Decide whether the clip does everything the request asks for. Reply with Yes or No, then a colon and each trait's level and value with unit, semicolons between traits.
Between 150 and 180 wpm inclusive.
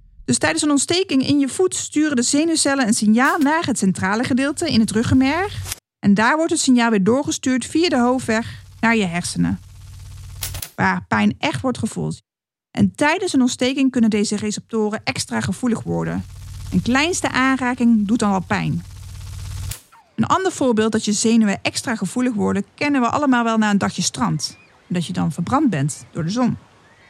Yes: average, 175 wpm